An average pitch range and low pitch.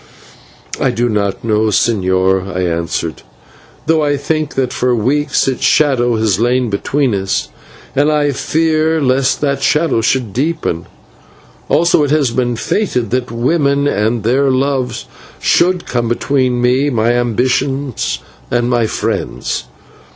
Yes: average, 4.1 semitones; low, 125 Hz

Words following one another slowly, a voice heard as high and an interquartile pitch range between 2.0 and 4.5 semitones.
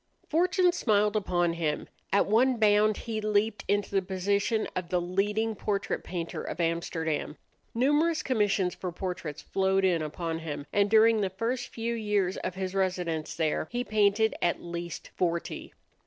No: average, 155 wpm; high, 195 Hz; average, 3.8 semitones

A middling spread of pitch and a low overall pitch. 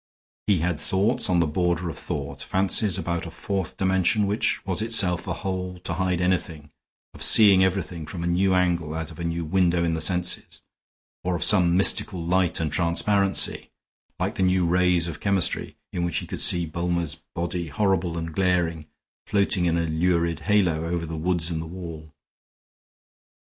No: narrow, 2.0 semitones; very low, 90 Hz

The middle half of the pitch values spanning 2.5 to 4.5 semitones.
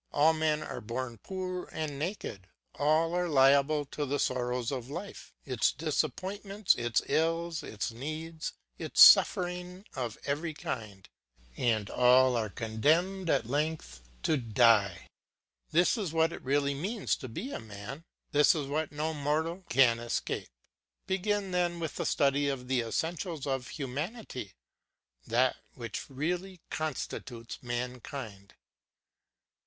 No: average, 5.2 semitones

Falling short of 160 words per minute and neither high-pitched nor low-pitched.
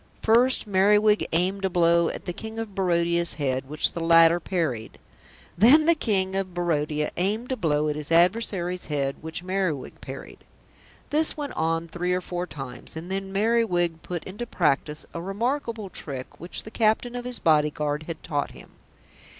No: average, 170 wpm; medium, 180 Hz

